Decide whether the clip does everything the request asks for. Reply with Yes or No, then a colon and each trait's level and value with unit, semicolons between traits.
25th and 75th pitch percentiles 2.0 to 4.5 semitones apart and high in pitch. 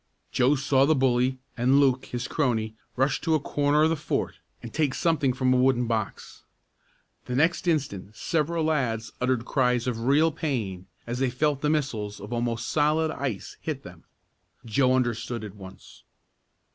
No: average, 3.9 semitones; low, 130 Hz